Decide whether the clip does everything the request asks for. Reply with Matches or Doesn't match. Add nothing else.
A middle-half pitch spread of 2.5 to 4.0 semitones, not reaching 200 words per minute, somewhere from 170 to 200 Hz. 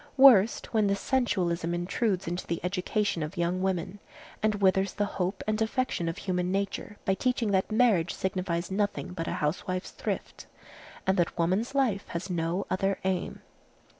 Matches